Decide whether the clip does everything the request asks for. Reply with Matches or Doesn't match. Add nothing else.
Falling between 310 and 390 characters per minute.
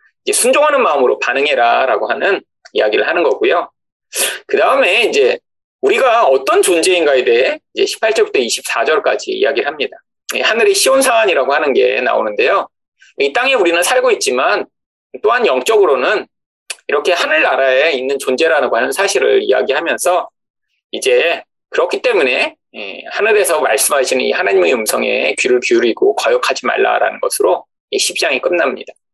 Matches